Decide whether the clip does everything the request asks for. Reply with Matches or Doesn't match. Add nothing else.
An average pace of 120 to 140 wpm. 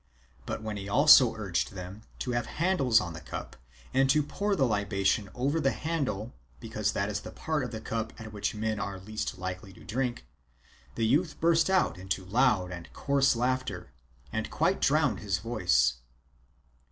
Doesn't match